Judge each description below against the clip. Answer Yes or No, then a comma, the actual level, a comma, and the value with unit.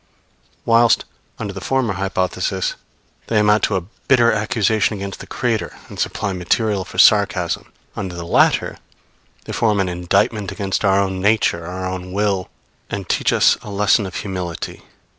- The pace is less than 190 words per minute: Yes, average, 160 wpm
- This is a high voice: No, low, 100 Hz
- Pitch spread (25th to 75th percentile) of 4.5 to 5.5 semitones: No, narrow, 2.4 semitones